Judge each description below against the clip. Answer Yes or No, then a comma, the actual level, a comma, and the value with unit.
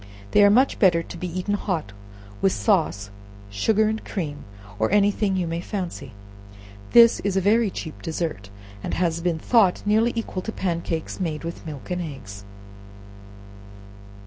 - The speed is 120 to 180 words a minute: Yes, average, 165 wpm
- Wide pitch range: No, average, 4.3 semitones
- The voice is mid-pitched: Yes, medium, 180 Hz